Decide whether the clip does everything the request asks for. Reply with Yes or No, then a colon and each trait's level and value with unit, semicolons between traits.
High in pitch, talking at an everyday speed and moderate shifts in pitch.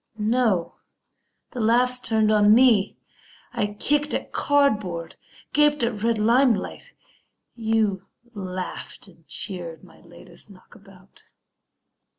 No: high, 215 Hz; slow, 105 wpm; average, 4.3 semitones